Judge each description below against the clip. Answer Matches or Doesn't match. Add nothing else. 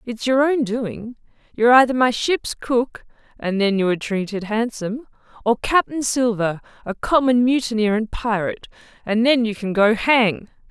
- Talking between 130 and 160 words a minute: Matches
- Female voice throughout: Matches